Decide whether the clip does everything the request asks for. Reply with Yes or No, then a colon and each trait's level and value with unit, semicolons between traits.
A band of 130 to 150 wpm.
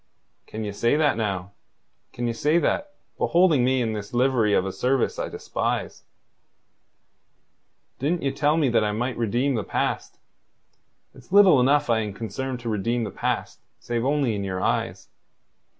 No: average, 165 wpm